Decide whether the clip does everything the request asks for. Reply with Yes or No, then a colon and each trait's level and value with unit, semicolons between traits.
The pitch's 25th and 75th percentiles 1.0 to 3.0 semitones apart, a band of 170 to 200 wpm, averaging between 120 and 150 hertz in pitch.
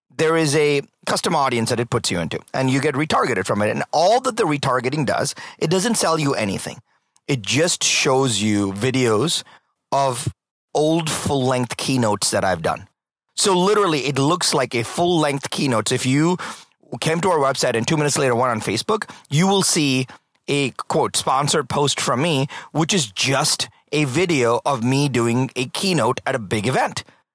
No: average, 4.1 semitones; average, 185 wpm; medium, 140 Hz